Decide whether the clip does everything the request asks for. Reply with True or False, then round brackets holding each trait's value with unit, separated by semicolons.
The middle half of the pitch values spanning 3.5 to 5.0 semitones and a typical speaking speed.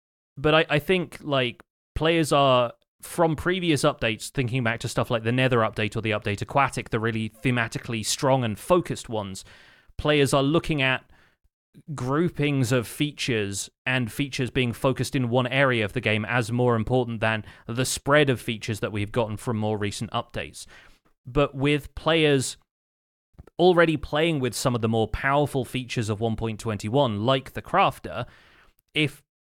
True (4.1 semitones; 160 wpm)